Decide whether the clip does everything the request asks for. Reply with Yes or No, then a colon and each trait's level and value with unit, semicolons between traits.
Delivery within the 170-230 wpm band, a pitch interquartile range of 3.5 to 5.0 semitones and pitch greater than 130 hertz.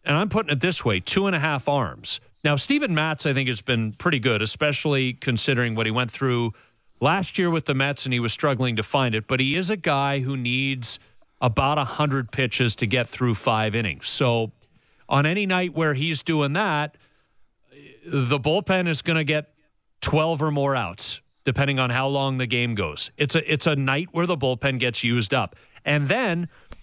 Yes: fast, 205 wpm; average, 3.9 semitones; medium, 140 Hz